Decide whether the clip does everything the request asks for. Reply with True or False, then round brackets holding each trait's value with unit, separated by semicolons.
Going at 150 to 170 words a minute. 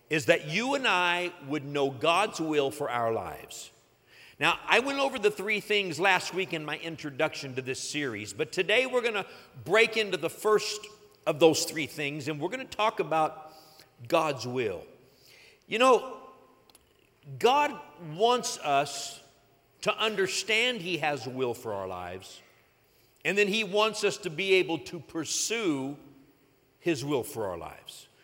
True (160 wpm)